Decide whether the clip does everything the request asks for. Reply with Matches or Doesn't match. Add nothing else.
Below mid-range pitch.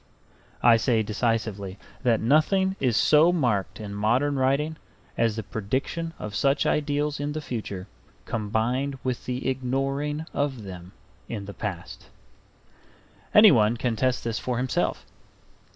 Matches